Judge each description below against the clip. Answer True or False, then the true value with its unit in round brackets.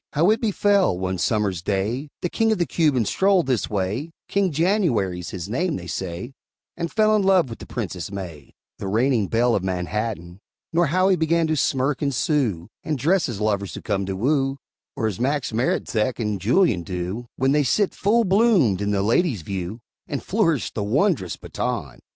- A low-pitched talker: True (125 Hz)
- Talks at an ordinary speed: True (190 wpm)